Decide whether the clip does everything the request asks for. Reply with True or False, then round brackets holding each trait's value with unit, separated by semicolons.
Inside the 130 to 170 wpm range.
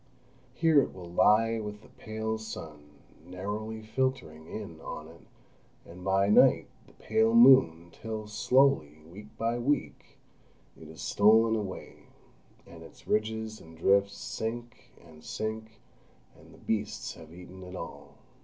True (140 wpm)